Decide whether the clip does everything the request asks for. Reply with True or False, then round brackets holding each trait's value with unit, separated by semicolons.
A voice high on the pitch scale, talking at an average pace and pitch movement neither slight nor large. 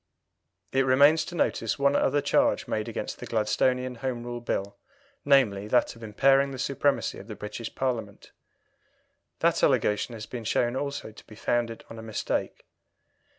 False (120 Hz; 160 wpm; 3.5 semitones)